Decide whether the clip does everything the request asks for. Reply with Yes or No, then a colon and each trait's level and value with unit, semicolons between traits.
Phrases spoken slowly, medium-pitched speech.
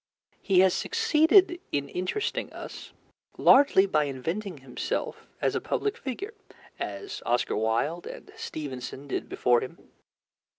Yes: slow, 125 wpm; medium, 175 Hz